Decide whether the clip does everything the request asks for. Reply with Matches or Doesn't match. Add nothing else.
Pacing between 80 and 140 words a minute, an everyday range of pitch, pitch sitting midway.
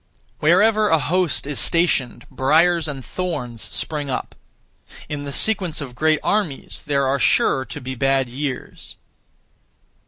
Matches